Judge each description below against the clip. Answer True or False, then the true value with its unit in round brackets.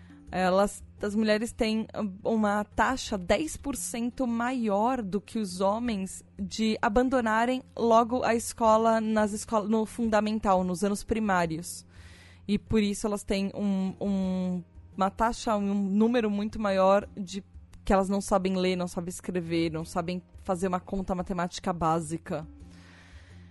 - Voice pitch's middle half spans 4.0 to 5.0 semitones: False (3.3 semitones)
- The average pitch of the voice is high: True (200 Hz)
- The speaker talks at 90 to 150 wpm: True (135 wpm)